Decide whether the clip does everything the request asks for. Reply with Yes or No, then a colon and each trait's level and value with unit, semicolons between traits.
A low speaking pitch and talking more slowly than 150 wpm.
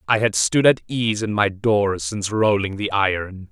No: low, 105 Hz; fast, 205 wpm